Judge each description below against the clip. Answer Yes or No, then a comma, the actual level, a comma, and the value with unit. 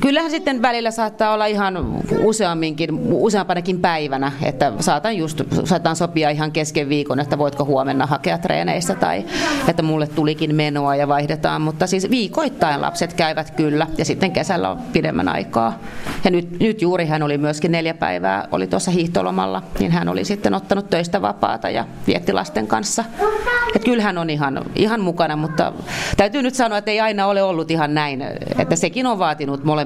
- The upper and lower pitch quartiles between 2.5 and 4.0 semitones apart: No, wide, 5.5 semitones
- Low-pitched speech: No, medium, 170 Hz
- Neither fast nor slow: No, fast, 170 wpm